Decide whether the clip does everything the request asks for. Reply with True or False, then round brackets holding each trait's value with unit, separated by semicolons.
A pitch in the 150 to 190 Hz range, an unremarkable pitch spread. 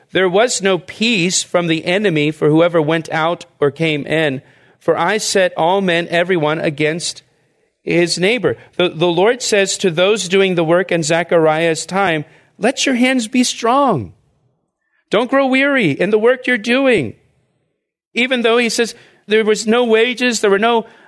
False (185 Hz; 5.8 semitones)